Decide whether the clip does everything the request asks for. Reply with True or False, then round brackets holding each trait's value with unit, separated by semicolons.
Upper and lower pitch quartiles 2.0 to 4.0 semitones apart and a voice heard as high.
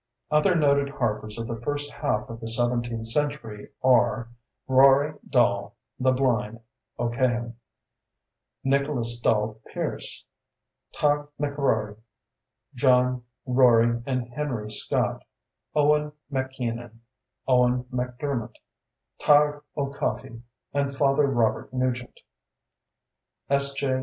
False (3.1 semitones; 125 Hz)